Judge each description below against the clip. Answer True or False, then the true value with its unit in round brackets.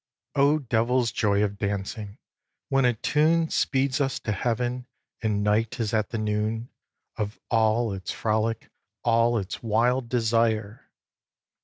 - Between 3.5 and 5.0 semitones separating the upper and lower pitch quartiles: False (2.7 semitones)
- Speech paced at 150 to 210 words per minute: False (140 wpm)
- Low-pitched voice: True (115 Hz)